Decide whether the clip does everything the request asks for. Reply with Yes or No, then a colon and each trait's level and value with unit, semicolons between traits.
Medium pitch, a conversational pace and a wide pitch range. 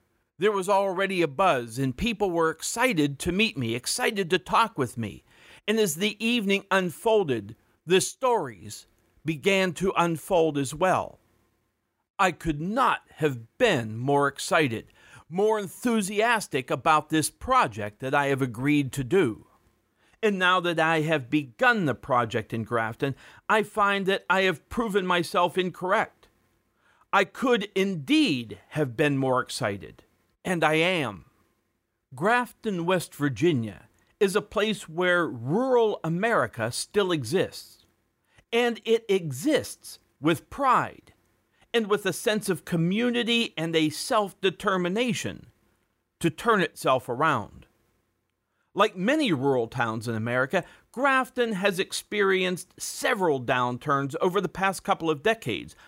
No: medium, 175 Hz; slow, 130 wpm; wide, 7.3 semitones